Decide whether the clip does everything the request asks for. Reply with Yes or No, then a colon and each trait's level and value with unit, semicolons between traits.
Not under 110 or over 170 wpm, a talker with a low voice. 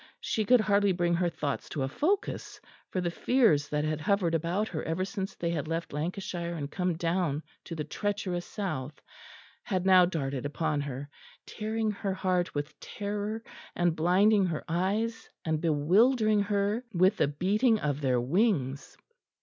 No: average, 165 wpm; medium, 175 Hz